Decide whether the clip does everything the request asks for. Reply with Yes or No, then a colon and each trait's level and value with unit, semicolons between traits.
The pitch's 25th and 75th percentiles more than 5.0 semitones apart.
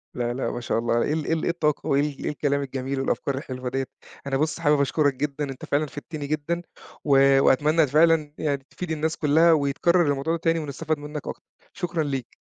No: narrow, 2.5 semitones